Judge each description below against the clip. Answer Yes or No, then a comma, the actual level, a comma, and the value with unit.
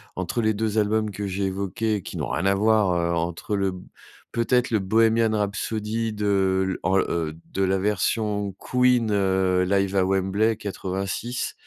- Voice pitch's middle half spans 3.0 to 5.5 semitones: No, narrow, 2.5 semitones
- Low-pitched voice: Yes, low, 100 Hz